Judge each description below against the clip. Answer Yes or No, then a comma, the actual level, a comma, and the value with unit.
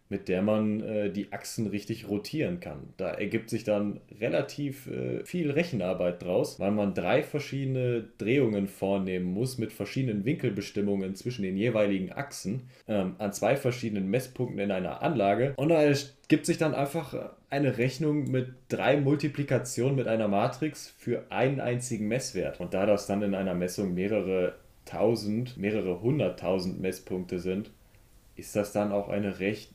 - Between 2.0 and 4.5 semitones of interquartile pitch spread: No, average, 4.9 semitones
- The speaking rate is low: No, average, 155 wpm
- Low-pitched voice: Yes, low, 110 Hz